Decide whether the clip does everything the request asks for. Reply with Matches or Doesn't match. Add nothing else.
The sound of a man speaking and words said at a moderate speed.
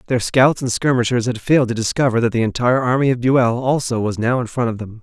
Doesn't match